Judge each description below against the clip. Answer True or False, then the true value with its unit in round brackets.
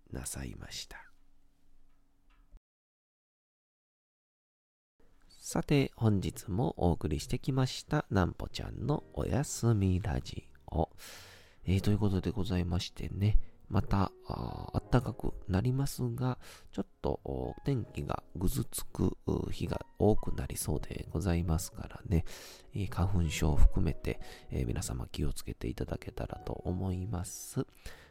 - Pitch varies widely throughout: False (4.9 semitones)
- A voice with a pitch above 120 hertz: False (95 Hz)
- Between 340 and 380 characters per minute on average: False (250 characters per minute)